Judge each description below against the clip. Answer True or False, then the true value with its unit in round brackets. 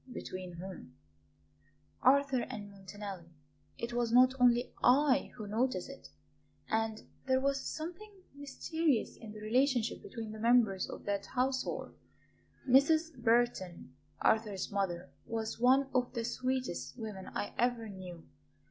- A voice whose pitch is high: True (235 Hz)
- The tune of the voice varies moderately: True (4.2 semitones)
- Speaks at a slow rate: True (130 wpm)